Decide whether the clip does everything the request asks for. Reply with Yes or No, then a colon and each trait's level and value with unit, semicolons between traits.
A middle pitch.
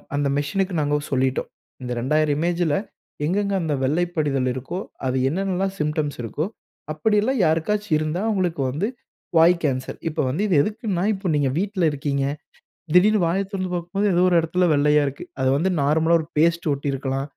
Yes: medium, 160 Hz